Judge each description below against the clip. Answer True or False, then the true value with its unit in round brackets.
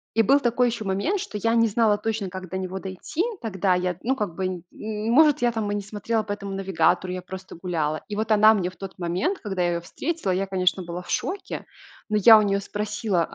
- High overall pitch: True (200 Hz)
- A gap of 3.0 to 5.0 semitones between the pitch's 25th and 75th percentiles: True (3.4 semitones)